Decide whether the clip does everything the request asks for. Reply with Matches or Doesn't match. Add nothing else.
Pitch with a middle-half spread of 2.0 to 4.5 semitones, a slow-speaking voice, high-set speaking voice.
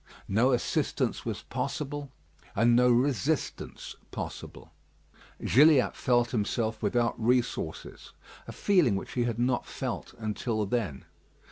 Doesn't match